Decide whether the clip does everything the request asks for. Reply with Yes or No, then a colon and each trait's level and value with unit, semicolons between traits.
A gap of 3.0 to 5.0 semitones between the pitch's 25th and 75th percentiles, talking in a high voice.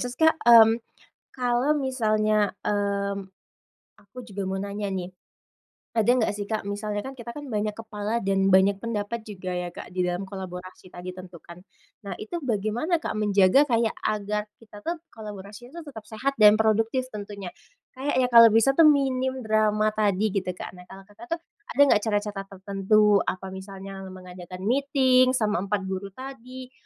Yes: average, 3.4 semitones; high, 210 Hz